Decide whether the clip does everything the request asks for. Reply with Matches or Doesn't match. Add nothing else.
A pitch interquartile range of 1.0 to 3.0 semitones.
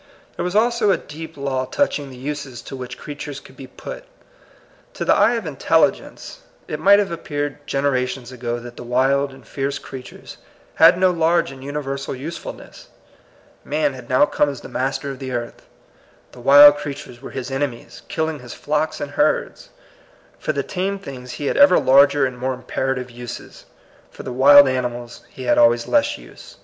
Matches